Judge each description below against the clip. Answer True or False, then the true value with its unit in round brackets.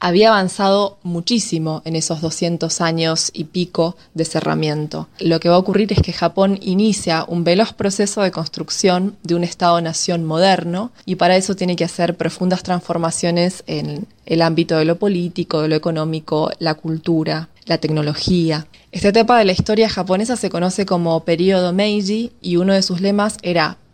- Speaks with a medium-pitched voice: True (175 Hz)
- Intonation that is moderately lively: True (3.0 semitones)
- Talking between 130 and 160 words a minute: False (170 wpm)